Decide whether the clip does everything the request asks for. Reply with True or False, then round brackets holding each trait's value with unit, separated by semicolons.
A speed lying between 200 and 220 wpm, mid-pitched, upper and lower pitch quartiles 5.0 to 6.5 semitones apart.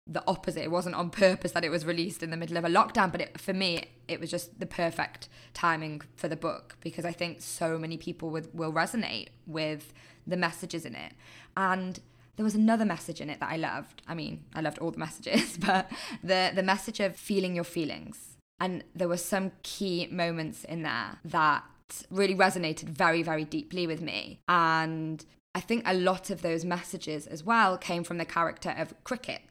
False (205 wpm; 175 Hz; 2.4 semitones)